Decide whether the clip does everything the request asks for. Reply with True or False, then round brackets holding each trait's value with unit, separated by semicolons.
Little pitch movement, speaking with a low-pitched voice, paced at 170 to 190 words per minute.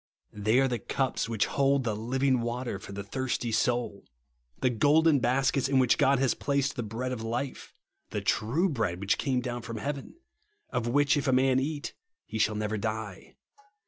False (3.5 semitones; 125 Hz; 185 wpm)